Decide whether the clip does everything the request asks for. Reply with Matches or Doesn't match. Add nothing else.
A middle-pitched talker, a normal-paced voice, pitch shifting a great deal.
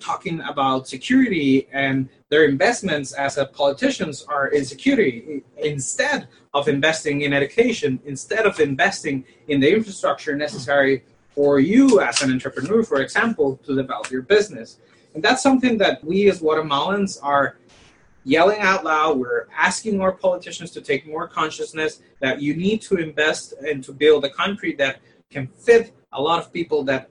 Matches